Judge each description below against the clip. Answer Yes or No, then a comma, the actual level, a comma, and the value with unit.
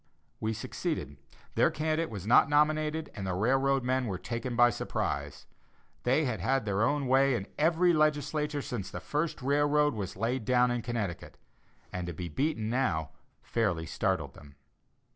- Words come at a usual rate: Yes, average, 160 wpm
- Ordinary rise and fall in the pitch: No, wide, 5.8 semitones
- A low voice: Yes, low, 125 Hz